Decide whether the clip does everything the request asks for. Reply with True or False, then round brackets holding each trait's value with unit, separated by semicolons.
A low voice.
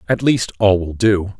True (100 Hz)